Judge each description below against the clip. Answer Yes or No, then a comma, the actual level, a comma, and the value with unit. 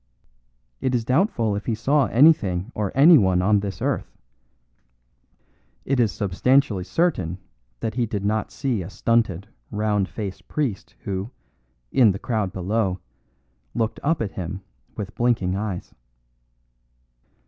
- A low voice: Yes, low, 105 Hz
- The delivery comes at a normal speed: No, slow, 130 wpm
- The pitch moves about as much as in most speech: Yes, average, 4.2 semitones